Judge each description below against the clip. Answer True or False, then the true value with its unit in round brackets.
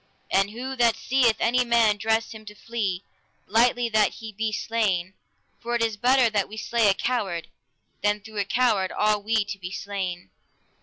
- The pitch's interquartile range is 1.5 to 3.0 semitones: True (2.6 semitones)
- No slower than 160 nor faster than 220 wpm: True (185 wpm)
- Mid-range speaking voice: False (220 Hz)